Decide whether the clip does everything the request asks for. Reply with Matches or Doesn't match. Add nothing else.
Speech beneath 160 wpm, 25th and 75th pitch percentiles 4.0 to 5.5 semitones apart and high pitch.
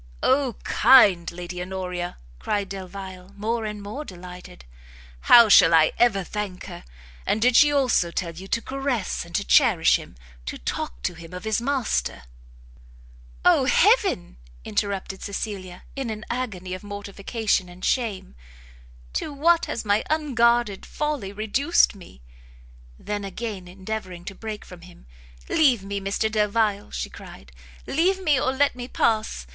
Matches